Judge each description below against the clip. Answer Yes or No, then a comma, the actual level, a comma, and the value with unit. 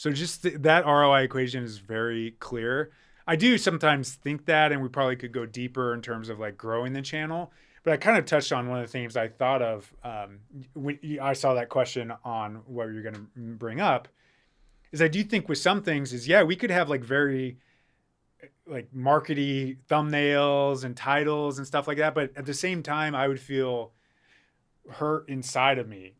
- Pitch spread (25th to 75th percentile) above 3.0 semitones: Yes, average, 3.7 semitones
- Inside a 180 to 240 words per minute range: Yes, average, 200 wpm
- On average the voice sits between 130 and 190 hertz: Yes, low, 135 Hz